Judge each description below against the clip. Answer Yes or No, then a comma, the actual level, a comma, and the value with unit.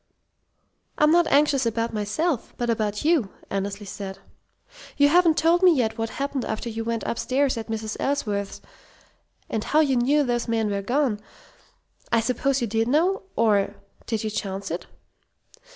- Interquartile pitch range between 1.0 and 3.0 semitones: No, average, 5.0 semitones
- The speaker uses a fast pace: No, average, 160 wpm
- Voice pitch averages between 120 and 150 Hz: No, high, 230 Hz